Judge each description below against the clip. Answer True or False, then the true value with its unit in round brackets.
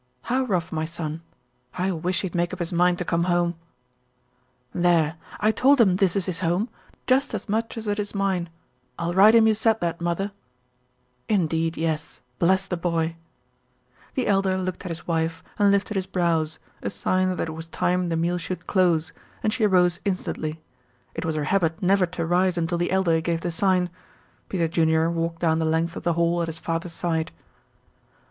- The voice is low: False (175 Hz)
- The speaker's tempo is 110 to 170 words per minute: False (195 wpm)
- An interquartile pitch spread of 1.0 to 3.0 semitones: True (2.5 semitones)